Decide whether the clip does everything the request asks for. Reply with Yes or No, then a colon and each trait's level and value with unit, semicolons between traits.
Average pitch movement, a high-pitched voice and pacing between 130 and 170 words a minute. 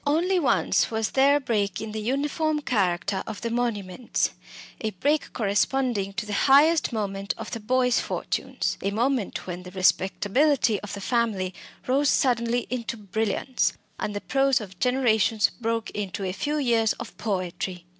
Yes: average, 4.7 semitones; high, 225 Hz; average, 160 wpm